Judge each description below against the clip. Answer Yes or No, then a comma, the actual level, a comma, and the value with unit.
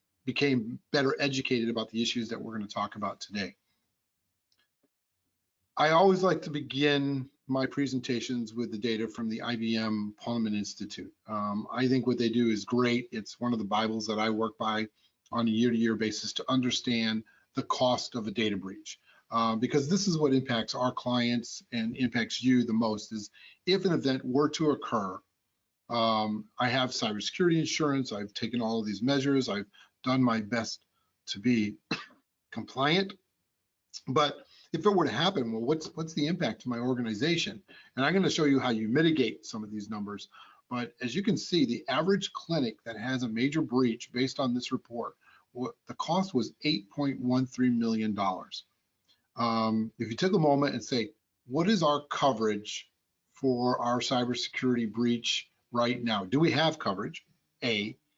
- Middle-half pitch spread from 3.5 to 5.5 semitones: Yes, average, 3.9 semitones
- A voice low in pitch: Yes, low, 120 Hz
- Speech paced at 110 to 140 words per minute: No, average, 175 wpm